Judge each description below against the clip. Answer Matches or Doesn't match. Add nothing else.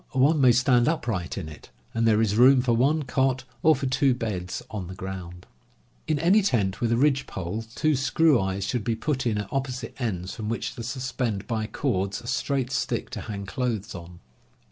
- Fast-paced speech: Matches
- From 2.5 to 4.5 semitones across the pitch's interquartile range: Doesn't match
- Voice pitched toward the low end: Matches